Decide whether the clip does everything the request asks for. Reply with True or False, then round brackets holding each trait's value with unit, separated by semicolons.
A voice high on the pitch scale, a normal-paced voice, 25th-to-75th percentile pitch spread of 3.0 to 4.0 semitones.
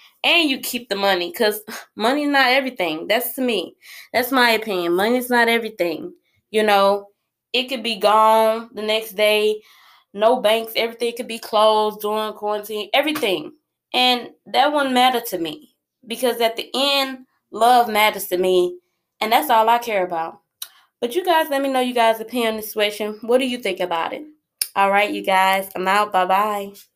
True (220 Hz; 180 wpm; 3.6 semitones)